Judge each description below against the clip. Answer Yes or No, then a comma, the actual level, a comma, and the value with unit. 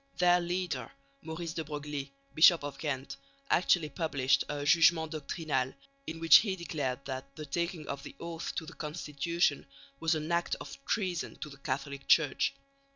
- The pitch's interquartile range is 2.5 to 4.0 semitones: Yes, average, 3.3 semitones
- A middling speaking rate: Yes, average, 160 wpm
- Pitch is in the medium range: Yes, medium, 155 Hz